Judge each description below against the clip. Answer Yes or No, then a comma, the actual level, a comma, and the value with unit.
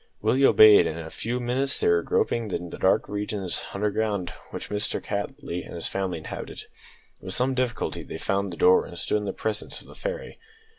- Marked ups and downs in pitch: No, average, 4.3 semitones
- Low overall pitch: Yes, low, 105 Hz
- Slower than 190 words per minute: No, fast, 205 wpm